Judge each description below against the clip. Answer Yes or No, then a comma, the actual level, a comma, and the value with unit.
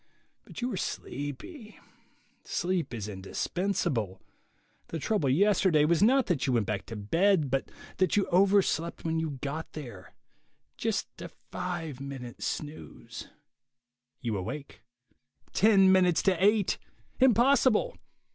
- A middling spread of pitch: No, wide, 6.7 semitones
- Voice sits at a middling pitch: Yes, medium, 165 Hz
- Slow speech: Yes, slow, 125 wpm